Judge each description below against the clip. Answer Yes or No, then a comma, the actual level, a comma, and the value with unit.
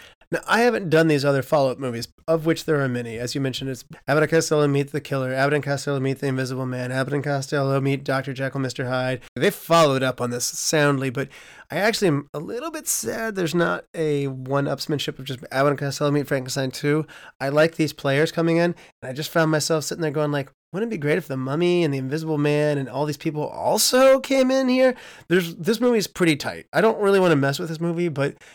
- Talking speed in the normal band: No, fast, 240 wpm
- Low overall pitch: No, medium, 150 Hz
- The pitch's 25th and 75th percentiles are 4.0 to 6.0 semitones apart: No, average, 3.4 semitones